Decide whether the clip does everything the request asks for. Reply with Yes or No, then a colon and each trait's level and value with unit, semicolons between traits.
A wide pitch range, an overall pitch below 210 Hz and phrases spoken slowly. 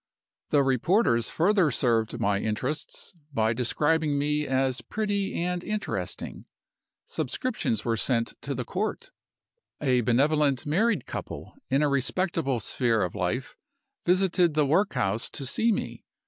Yes: wide, 6.7 semitones; medium, 140 Hz; slow, 130 wpm